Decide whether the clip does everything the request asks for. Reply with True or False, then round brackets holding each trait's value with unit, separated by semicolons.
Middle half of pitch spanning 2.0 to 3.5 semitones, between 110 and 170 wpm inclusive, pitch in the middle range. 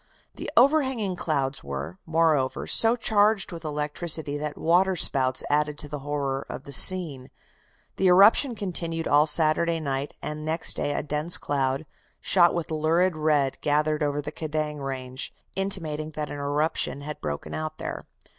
True (2.9 semitones; 155 wpm; 155 Hz)